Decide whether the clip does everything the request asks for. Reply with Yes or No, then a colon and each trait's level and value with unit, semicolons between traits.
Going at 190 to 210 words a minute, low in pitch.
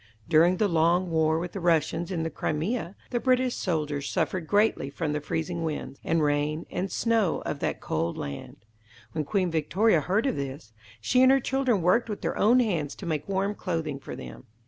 No: average, 195 wpm; medium, 170 Hz